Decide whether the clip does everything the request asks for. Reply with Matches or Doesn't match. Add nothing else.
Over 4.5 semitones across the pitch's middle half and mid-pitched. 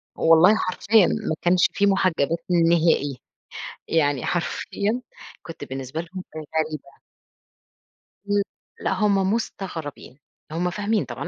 Doesn't match